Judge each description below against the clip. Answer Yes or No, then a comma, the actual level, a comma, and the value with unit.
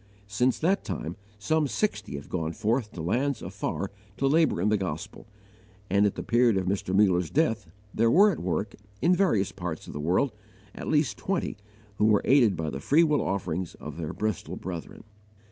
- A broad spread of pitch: Yes, wide, 7.3 semitones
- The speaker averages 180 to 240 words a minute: Yes, average, 190 wpm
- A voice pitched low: Yes, low, 105 Hz